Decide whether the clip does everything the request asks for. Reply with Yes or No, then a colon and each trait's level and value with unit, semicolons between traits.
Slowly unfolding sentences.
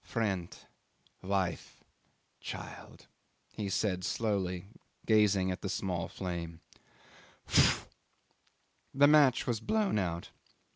Yes: slow, 95 wpm